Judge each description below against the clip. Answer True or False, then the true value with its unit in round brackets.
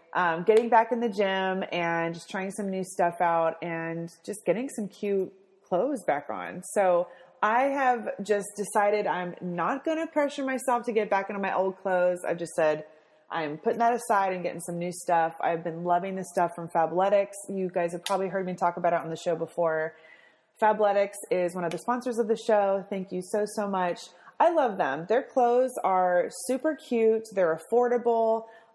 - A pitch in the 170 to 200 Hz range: True (190 Hz)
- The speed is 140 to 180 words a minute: False (200 wpm)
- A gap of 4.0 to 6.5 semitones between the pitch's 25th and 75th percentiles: True (4.4 semitones)